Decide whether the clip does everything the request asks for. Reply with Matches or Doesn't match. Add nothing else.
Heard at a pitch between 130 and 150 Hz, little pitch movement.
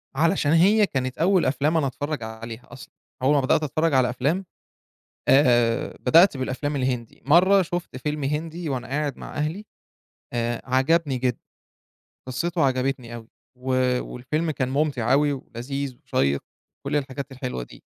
Doesn't match